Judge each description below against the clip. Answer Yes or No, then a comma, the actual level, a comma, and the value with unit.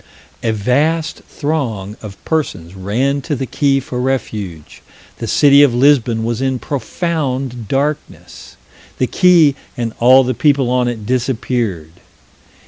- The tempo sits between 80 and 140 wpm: Yes, slow, 135 wpm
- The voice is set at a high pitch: No, low, 130 Hz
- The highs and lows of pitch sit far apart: No, average, 4.0 semitones